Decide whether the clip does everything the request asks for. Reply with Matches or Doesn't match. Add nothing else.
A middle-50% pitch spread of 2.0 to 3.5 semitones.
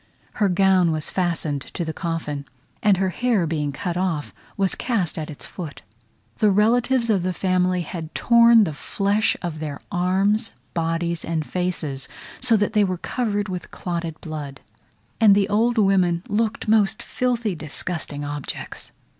Doesn't match